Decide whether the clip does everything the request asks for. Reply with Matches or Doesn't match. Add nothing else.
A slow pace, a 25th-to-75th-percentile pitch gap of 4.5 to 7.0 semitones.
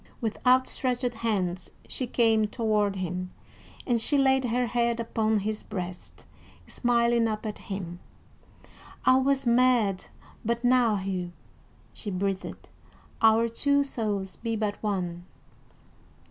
Doesn't match